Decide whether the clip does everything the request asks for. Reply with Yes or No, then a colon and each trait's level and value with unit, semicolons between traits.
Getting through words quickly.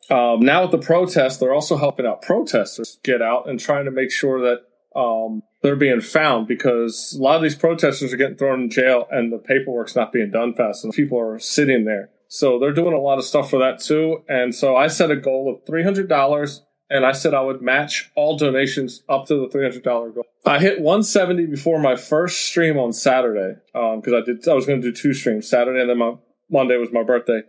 Yes: fast, 240 wpm